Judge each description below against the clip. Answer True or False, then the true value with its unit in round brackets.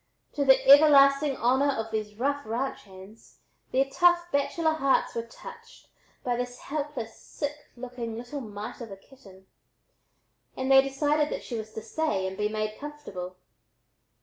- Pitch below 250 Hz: False (260 Hz)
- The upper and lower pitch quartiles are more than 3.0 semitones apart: True (4.7 semitones)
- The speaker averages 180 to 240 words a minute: False (155 wpm)